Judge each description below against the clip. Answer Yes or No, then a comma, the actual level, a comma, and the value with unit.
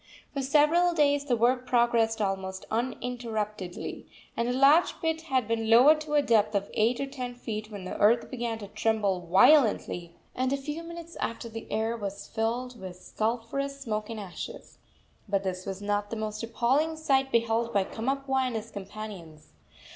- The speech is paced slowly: No, average, 175 wpm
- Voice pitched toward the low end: No, high, 230 Hz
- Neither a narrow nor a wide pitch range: Yes, average, 4.2 semitones